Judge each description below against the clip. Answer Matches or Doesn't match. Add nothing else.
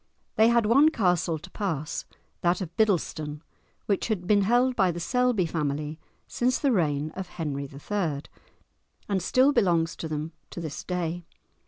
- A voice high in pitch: Doesn't match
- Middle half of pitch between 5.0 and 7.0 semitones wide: Matches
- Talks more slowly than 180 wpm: Matches